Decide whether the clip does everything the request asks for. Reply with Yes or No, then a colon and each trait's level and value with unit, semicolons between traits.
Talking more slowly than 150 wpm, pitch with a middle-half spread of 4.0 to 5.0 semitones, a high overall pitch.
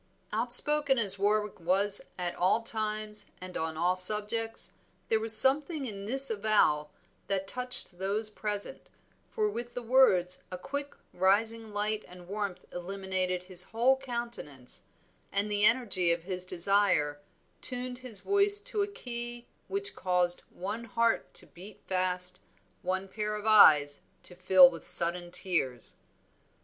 Yes: average, 140 wpm; average, 4.3 semitones; high, 205 Hz